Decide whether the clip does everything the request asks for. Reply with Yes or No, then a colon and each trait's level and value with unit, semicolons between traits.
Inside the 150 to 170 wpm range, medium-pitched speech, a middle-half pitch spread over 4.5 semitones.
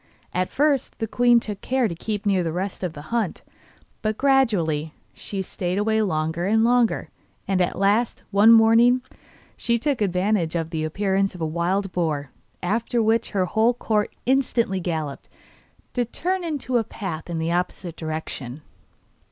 No: average, 165 wpm; high, 200 Hz; average, 5.2 semitones